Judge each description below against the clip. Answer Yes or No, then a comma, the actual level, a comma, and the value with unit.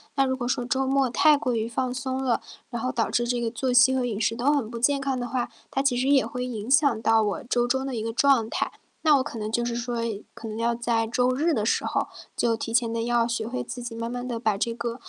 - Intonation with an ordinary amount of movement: No, narrow, 2.2 semitones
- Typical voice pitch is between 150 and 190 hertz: No, high, 240 Hz